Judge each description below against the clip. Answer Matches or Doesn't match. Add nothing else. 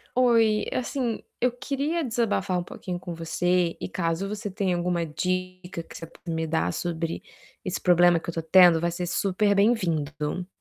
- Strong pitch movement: Doesn't match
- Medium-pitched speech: Matches